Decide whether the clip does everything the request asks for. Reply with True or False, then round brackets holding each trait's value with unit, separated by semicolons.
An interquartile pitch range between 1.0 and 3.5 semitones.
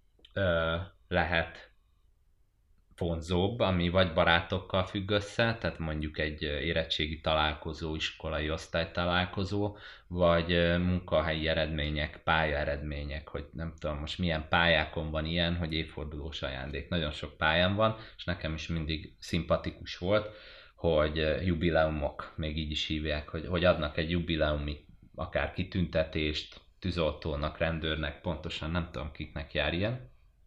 True (2.4 semitones)